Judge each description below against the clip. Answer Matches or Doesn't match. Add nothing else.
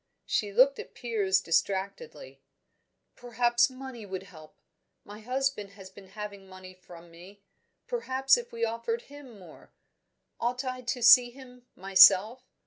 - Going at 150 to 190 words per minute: Doesn't match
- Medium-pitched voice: Doesn't match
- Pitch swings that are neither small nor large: Matches